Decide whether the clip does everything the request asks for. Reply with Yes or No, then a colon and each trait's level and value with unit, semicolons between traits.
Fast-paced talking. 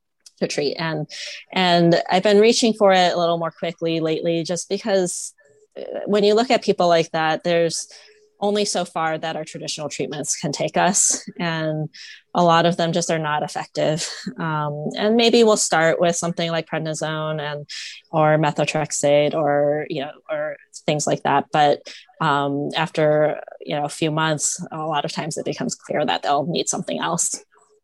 No: average, 175 wpm